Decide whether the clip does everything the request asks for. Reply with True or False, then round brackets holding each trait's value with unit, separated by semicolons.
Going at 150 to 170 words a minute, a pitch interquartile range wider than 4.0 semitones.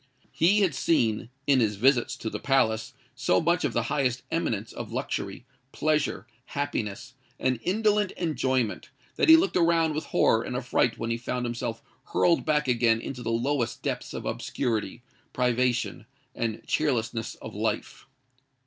True (155 wpm; 4.8 semitones)